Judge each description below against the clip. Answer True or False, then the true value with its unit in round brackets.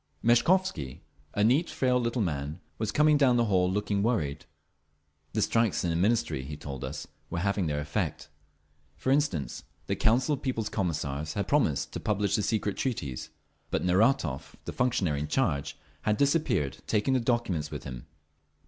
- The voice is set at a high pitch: False (105 Hz)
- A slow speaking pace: False (165 wpm)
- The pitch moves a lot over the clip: True (8.4 semitones)